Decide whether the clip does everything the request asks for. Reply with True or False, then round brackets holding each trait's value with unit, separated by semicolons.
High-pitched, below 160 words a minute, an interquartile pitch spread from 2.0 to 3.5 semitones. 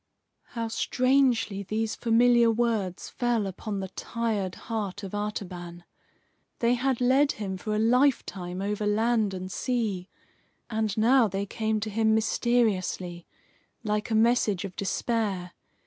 True (215 Hz; 135 wpm; 3.2 semitones)